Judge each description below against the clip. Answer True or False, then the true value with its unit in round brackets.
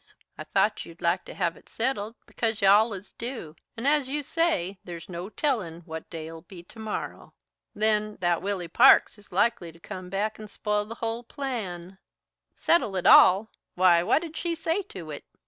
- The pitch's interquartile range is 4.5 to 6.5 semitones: True (4.9 semitones)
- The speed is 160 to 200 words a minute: True (185 wpm)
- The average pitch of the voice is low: False (205 Hz)